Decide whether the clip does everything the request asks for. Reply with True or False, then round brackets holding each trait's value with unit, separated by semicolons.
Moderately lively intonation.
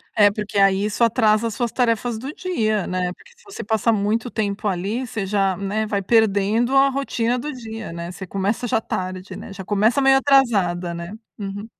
True (3.3 semitones)